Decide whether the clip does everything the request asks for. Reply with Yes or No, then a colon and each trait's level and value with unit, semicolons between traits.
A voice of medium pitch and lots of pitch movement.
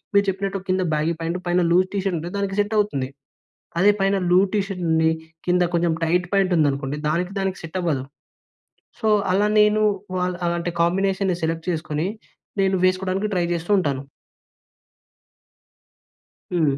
No: medium, 180 Hz; average, 2.9 semitones